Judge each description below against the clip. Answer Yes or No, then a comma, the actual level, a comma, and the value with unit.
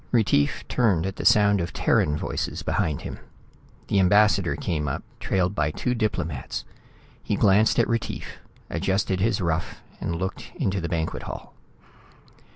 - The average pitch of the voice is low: Yes, very low, 95 Hz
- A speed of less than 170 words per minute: Yes, average, 150 wpm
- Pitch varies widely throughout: No, average, 3.8 semitones